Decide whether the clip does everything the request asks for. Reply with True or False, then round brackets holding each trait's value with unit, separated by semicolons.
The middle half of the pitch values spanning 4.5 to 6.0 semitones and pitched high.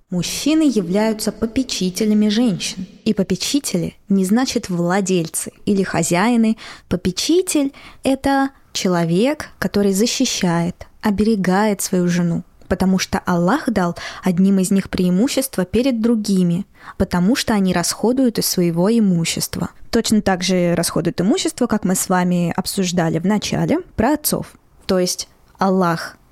False (4.1 semitones; 195 Hz)